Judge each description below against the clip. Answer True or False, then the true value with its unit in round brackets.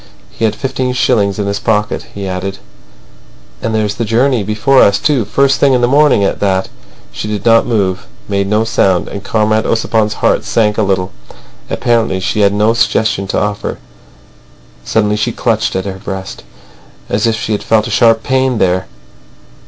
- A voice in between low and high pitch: False (105 Hz)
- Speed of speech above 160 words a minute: True (175 wpm)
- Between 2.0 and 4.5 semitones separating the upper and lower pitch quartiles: True (2.5 semitones)